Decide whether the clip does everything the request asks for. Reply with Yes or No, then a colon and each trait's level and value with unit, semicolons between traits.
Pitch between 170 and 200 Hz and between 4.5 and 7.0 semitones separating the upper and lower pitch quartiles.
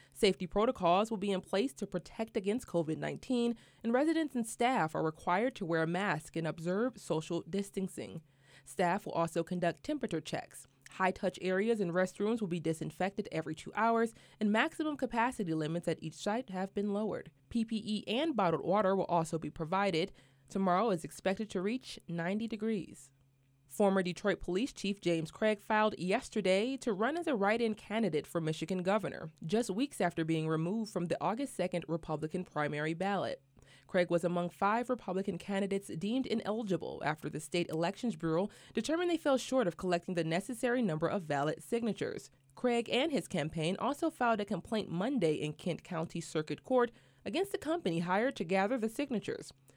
Yes: high, 190 Hz; average, 5.0 semitones